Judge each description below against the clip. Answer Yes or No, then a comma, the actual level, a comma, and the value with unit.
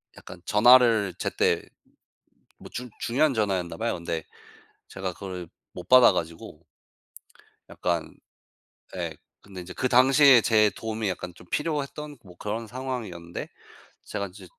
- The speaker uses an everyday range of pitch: No, wide, 5.7 semitones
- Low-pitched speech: Yes, low, 105 Hz